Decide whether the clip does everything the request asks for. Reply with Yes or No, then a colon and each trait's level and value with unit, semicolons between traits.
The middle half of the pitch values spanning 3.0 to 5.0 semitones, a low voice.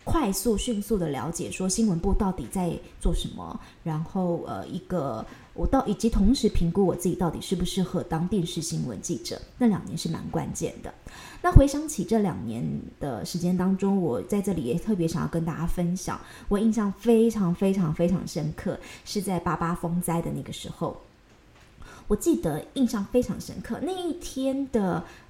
No: average, 4.1 semitones; medium, 185 Hz